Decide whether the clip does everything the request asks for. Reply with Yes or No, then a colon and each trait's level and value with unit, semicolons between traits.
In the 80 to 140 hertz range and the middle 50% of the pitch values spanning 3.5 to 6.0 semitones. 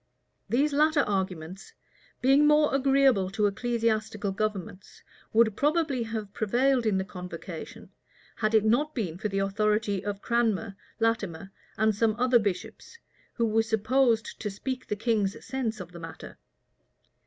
No: high, 220 Hz; average, 3.9 semitones